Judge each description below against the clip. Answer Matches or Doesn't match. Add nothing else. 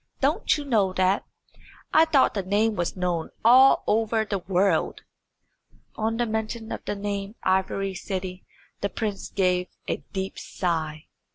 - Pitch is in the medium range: Doesn't match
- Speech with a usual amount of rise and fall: Matches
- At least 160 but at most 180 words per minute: Doesn't match